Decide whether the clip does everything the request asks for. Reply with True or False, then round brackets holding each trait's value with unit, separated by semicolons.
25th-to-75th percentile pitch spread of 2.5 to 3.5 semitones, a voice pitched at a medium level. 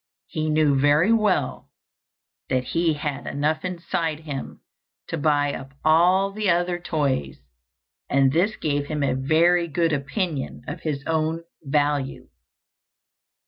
True (3.0 semitones; 155 Hz)